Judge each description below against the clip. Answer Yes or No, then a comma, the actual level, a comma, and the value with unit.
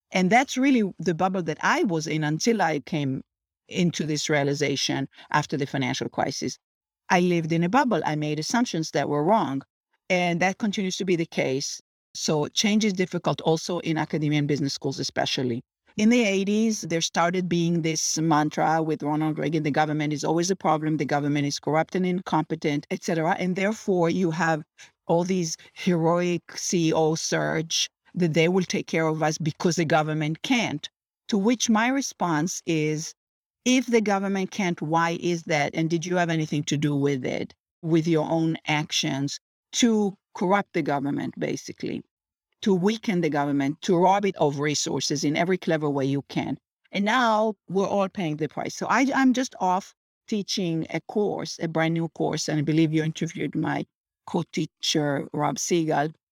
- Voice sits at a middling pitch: Yes, medium, 165 Hz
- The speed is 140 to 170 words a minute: No, average, 180 wpm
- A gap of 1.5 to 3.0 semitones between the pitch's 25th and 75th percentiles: No, average, 3.7 semitones